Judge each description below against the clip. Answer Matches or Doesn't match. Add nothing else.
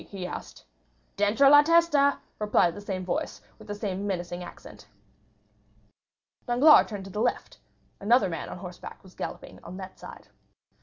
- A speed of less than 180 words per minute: Matches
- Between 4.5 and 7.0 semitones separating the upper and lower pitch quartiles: Matches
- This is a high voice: Matches